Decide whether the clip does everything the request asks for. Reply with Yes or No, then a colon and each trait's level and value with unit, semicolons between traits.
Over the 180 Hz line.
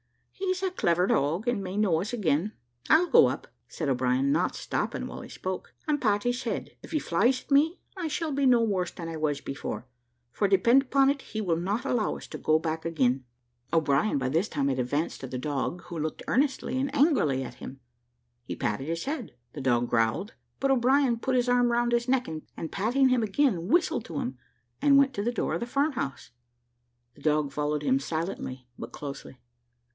Yes: high, 190 Hz